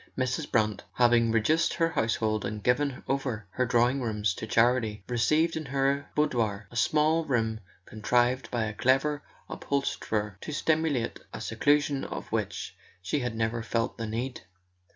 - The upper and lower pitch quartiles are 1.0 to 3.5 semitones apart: No, average, 4.0 semitones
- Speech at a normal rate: Yes, average, 150 wpm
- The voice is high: No, low, 120 Hz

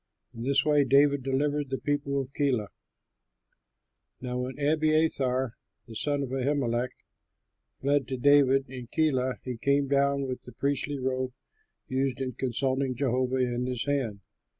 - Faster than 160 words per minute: No, average, 145 wpm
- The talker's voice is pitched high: No, low, 135 Hz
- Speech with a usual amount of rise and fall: No, narrow, 1.9 semitones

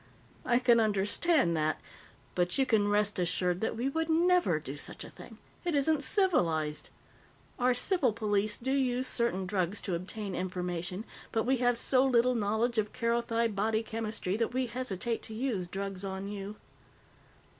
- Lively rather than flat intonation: No, average, 4.5 semitones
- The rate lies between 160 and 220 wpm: Yes, average, 165 wpm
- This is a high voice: Yes, high, 220 Hz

